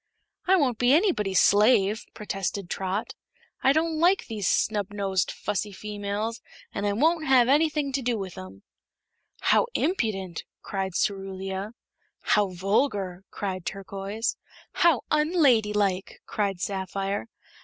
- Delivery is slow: Yes, slow, 120 wpm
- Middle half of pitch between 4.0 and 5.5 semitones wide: Yes, average, 4.9 semitones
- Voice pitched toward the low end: No, high, 205 Hz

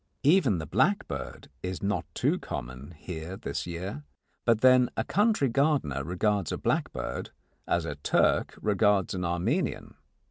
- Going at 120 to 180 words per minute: Yes, average, 140 wpm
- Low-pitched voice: Yes, very low, 95 Hz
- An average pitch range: No, wide, 6.8 semitones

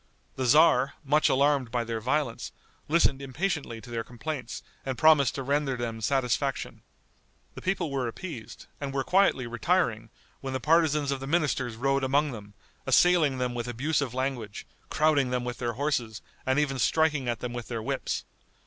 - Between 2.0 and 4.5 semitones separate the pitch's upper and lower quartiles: Yes, average, 3.7 semitones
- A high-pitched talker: No, low, 135 Hz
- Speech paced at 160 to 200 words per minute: Yes, average, 170 wpm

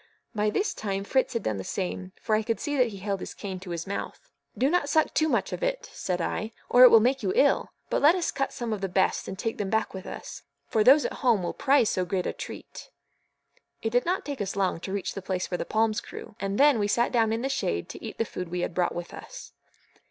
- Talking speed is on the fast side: Yes, fast, 270 wpm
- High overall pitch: Yes, high, 215 Hz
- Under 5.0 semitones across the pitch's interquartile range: No, average, 5.3 semitones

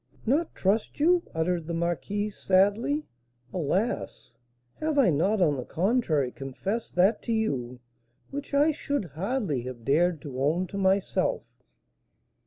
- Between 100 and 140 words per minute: Yes, slow, 135 wpm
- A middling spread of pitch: No, wide, 7.3 semitones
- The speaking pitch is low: No, medium, 185 Hz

